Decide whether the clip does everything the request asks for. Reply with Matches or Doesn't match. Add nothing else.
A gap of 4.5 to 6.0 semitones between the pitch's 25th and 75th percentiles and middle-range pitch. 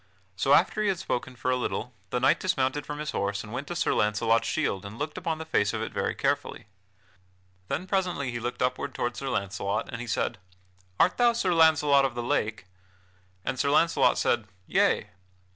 Doesn't match